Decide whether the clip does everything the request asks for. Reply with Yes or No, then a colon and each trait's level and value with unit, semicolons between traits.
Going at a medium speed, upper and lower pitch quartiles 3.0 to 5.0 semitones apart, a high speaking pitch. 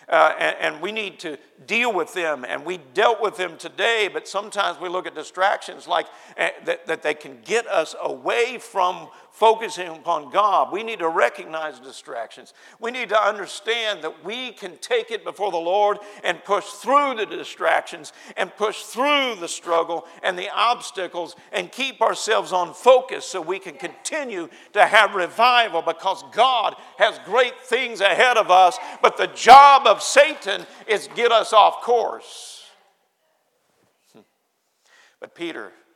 No: average, 160 wpm; wide, 5.6 semitones; high, 210 Hz